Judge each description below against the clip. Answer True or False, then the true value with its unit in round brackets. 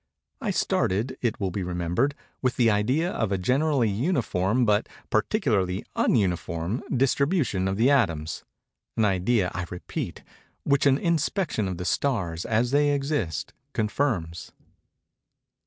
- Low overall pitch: True (110 Hz)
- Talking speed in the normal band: False (125 wpm)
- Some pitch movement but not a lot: False (6.9 semitones)